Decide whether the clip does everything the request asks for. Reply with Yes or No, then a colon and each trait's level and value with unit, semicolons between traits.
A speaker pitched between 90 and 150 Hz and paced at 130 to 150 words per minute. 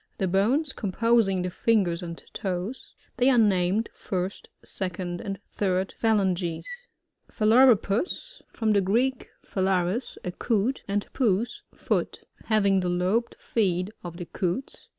No: high, 195 Hz; average, 140 wpm